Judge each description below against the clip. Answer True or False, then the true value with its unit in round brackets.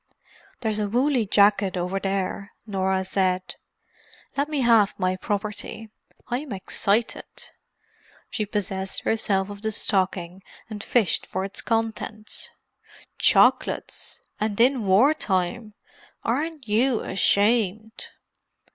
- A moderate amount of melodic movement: True (3.0 semitones)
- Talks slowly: True (100 wpm)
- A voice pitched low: False (210 Hz)